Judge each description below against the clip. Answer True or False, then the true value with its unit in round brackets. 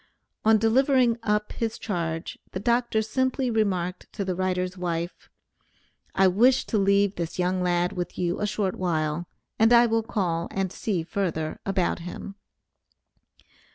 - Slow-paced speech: False (150 wpm)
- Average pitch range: True (3.9 semitones)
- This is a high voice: True (195 Hz)